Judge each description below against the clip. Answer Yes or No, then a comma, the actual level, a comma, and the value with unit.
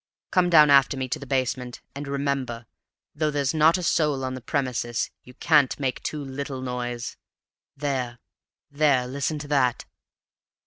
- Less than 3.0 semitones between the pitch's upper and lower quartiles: Yes, narrow, 2.5 semitones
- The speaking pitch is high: No, low, 135 Hz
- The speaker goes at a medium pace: Yes, average, 160 wpm